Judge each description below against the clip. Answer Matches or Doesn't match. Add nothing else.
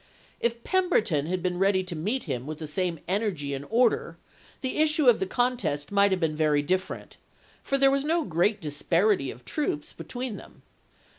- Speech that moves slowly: Doesn't match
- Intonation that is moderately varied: Doesn't match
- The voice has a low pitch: Doesn't match